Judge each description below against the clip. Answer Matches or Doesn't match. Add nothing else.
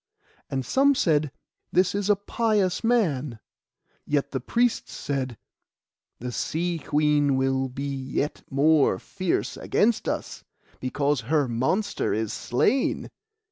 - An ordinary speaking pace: Doesn't match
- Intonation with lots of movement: Matches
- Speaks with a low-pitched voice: Doesn't match